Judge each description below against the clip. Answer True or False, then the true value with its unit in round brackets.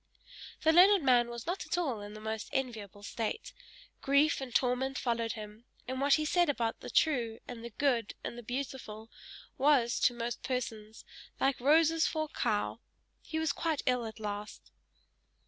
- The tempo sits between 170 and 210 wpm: True (175 wpm)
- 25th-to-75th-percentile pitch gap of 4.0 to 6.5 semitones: True (4.3 semitones)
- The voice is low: False (250 Hz)